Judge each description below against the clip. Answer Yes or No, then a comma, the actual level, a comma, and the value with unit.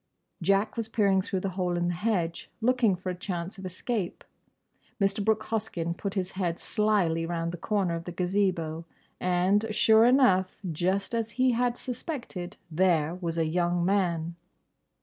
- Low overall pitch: No, medium, 185 Hz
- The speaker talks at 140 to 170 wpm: Yes, average, 155 wpm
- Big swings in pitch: No, average, 3.6 semitones